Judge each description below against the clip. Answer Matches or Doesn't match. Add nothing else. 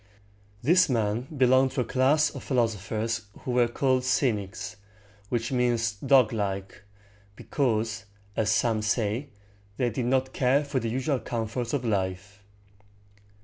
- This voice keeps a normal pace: Doesn't match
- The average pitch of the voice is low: Matches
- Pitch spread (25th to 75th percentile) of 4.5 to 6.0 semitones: Doesn't match